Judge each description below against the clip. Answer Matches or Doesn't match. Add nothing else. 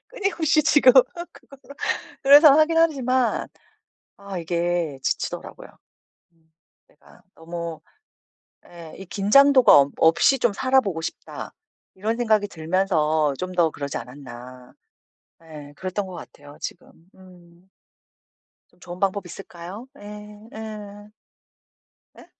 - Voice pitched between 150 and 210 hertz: Matches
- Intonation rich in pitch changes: Matches